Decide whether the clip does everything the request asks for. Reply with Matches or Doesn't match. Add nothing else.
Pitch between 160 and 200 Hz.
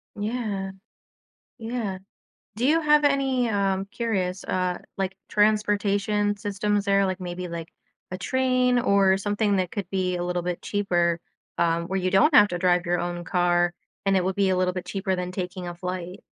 Matches